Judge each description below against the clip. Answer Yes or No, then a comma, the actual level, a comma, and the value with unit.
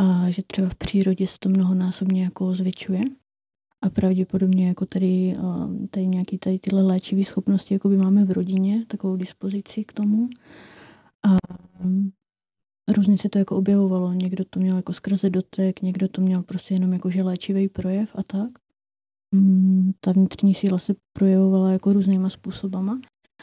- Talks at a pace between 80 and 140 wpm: No, average, 150 wpm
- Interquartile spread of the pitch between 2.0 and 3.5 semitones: No, narrow, 1.1 semitones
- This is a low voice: No, high, 190 Hz